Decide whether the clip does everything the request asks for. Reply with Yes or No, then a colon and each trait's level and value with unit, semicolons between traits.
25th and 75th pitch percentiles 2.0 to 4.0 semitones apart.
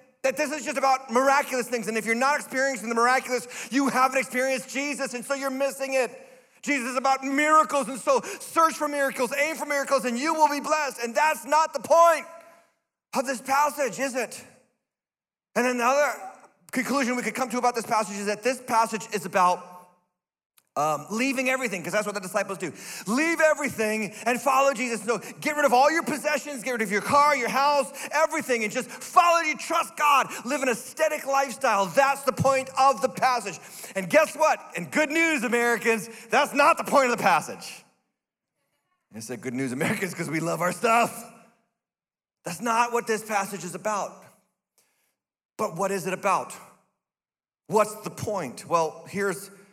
No: average, 4.5 semitones